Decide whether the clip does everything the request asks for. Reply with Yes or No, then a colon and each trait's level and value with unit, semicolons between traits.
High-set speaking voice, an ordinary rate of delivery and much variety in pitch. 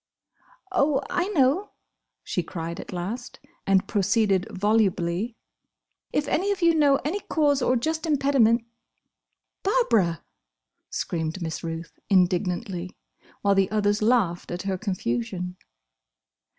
No: high, 210 Hz; slow, 120 wpm; wide, 7.6 semitones